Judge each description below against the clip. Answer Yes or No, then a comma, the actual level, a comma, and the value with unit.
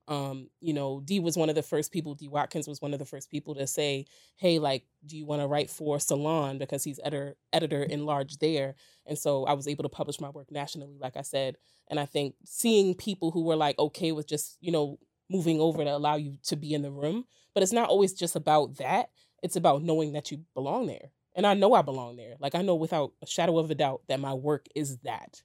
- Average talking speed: No, fast, 250 wpm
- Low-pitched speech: No, medium, 150 Hz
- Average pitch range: No, narrow, 2.3 semitones